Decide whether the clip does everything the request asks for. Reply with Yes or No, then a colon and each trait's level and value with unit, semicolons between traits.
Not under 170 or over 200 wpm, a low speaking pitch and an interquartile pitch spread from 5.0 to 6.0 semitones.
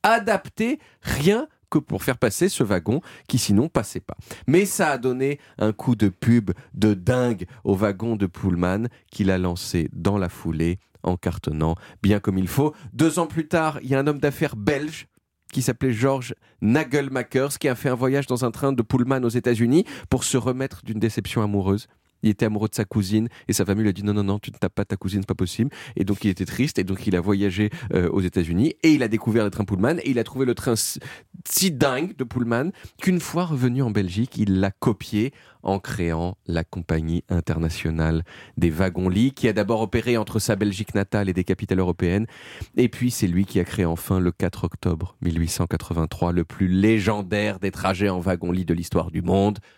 No: average, 210 wpm; low, 105 Hz; wide, 5.4 semitones